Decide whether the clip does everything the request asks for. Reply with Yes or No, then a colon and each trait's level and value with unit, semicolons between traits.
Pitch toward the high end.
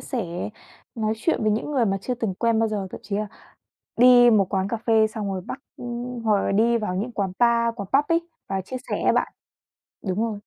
Yes: high, 220 Hz